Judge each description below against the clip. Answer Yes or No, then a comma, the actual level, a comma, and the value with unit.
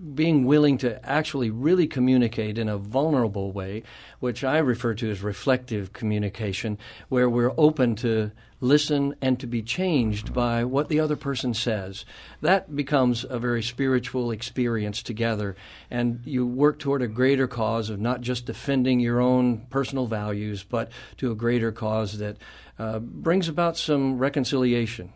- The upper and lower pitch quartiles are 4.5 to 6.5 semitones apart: No, average, 3.7 semitones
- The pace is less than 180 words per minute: Yes, average, 155 wpm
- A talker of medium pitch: No, low, 120 Hz